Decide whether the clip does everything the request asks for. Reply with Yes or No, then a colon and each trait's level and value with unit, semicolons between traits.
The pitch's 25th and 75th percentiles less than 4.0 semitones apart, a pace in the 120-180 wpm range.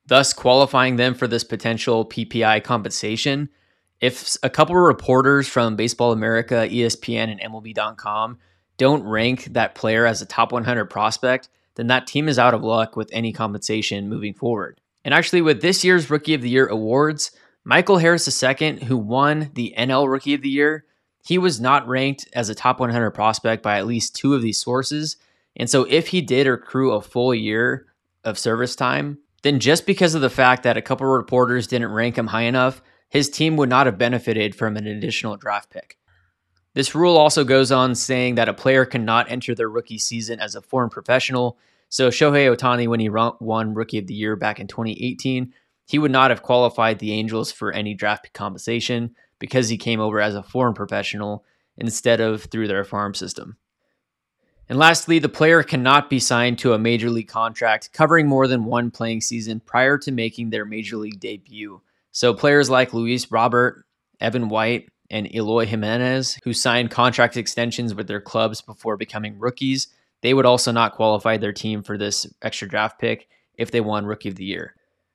No: average, 3.0 semitones; average, 190 wpm